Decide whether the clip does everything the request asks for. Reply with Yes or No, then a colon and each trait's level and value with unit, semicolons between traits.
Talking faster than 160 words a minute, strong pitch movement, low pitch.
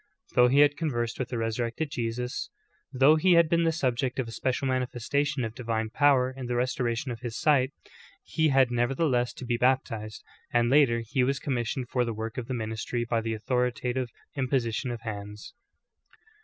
No: average, 185 wpm; narrow, 2.4 semitones; low, 125 Hz